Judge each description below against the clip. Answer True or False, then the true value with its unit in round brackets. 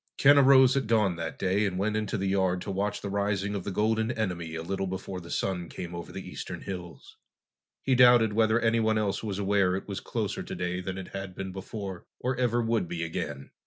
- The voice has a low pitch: True (100 Hz)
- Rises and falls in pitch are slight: False (3.2 semitones)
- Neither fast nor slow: False (220 wpm)